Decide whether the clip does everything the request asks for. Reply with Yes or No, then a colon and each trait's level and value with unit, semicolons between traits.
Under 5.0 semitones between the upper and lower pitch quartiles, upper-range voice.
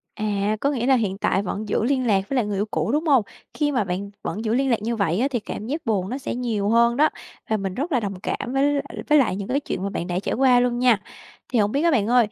Yes: average, 4.6 semitones; high, 230 Hz